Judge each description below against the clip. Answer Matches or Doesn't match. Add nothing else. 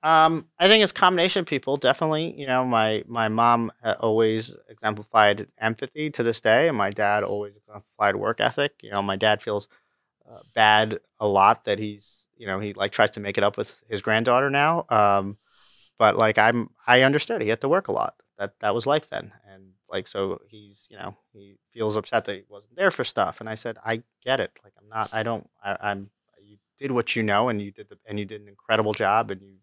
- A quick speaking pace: Matches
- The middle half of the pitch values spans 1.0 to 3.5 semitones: Matches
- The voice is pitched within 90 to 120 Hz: Matches